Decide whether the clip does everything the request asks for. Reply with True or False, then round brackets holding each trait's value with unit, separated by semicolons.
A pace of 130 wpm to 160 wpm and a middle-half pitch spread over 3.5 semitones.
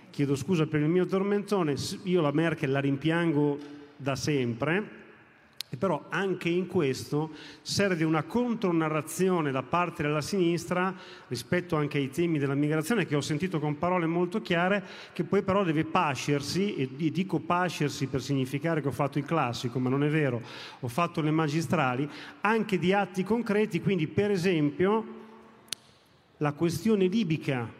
True (155 wpm; 4.1 semitones)